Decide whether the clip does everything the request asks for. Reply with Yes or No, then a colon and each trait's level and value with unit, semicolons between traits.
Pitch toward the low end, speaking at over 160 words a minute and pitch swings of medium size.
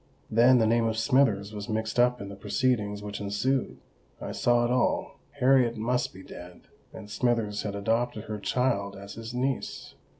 Yes: low, 115 Hz; average, 170 wpm; average, 3.2 semitones